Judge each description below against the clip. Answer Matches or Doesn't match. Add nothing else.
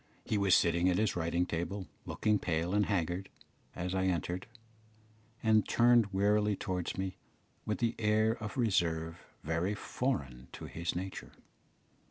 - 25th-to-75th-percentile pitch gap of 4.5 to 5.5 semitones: Doesn't match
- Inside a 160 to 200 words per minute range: Doesn't match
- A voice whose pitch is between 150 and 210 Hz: Doesn't match